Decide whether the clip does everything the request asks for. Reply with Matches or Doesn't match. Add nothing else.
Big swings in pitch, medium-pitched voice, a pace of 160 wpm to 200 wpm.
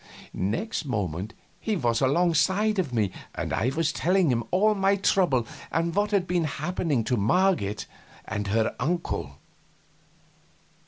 Doesn't match